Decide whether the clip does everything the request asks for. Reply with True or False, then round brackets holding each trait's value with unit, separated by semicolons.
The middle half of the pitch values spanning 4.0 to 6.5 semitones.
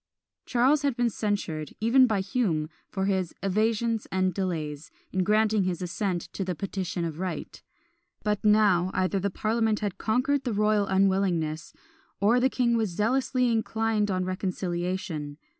False (3.4 semitones)